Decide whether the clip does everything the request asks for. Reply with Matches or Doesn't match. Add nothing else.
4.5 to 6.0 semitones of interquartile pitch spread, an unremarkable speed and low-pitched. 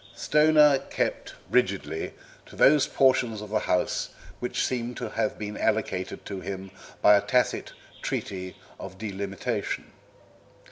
Doesn't match